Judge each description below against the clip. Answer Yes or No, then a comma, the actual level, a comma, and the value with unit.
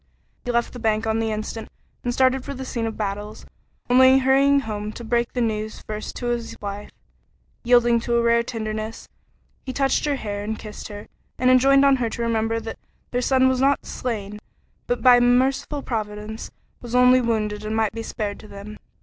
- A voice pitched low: No, high, 235 Hz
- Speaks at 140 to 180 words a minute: No, average, 200 wpm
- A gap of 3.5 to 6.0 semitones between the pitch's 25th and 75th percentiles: No, average, 2.9 semitones